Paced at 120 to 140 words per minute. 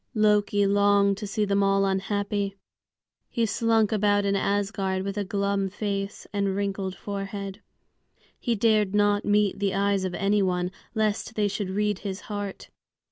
No: average, 155 wpm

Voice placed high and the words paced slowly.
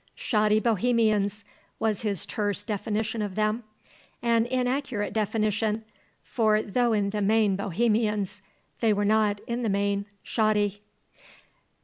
Yes: high, 215 Hz; slow, 120 wpm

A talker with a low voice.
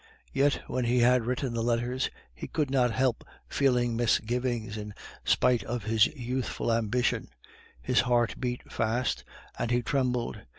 Yes: low, 120 Hz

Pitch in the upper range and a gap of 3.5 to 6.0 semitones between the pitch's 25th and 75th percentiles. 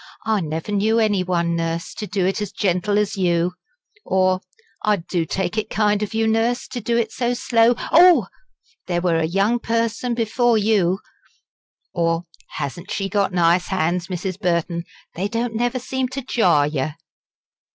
Yes: high, 200 Hz; average, 4.6 semitones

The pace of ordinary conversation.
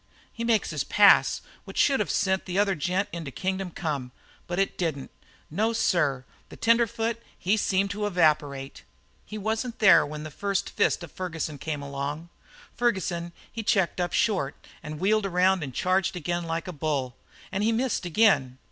Yes: average, 170 wpm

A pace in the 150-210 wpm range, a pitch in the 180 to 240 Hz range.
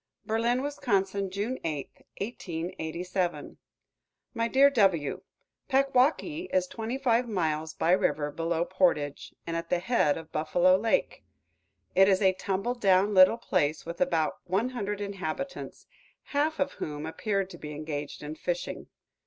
No: average, 140 wpm; high, 190 Hz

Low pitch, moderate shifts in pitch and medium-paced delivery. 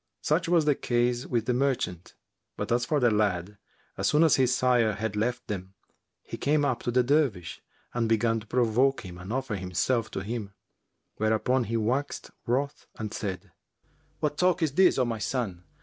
Yes: low, 120 Hz; average, 4.1 semitones; average, 185 wpm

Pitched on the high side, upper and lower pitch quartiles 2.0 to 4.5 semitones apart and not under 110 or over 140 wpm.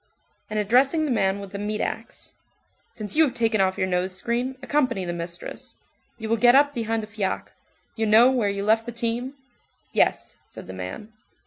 No: high, 220 Hz; average, 3.5 semitones; average, 195 wpm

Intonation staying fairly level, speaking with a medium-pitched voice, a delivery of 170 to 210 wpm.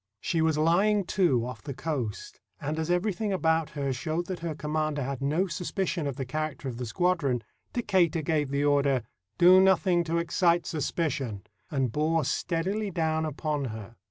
No: average, 3.8 semitones; medium, 155 Hz; average, 175 wpm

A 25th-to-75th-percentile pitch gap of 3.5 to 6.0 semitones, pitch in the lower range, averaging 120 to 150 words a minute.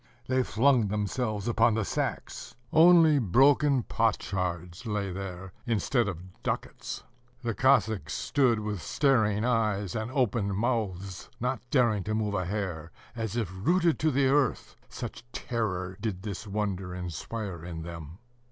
Yes: average, 4.6 semitones; low, 105 Hz; average, 140 wpm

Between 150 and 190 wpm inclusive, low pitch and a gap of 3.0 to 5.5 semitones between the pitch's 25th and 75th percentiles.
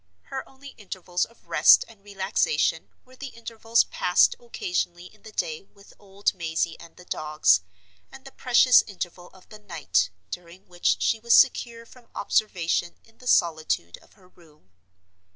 No: average, 160 wpm; high, 195 Hz; average, 5.1 semitones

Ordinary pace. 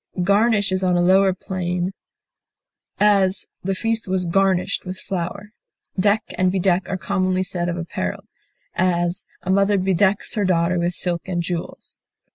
Yes: average, 150 wpm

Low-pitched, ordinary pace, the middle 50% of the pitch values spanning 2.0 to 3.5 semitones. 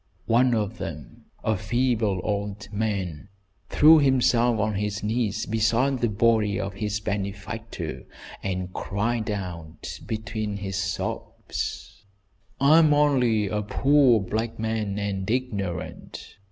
No: low, 105 Hz; slow, 120 wpm; average, 2.9 semitones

